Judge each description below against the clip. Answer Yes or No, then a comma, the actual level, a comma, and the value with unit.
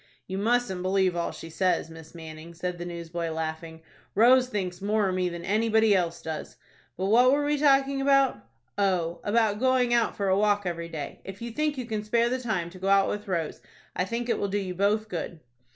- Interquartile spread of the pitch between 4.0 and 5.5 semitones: Yes, average, 5.2 semitones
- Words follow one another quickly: Yes, fast, 215 wpm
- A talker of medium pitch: No, high, 195 Hz